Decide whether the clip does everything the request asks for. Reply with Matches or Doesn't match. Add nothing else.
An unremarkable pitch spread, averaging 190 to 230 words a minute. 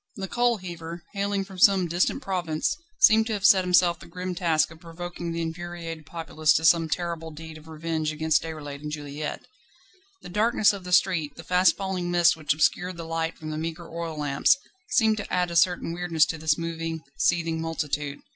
Doesn't match